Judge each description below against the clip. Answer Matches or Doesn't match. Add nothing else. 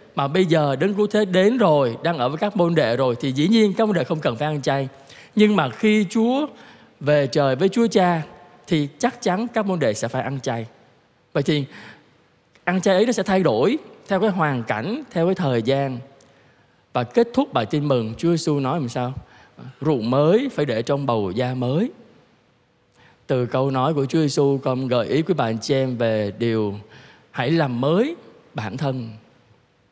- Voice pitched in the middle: Matches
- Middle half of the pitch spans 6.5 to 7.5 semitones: Matches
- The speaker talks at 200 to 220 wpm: Matches